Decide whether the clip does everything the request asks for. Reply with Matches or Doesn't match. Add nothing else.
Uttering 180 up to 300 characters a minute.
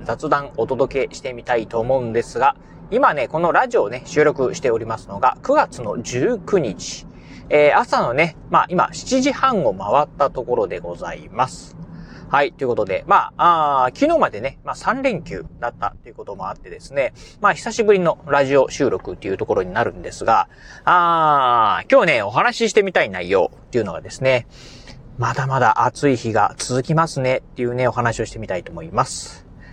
Doesn't match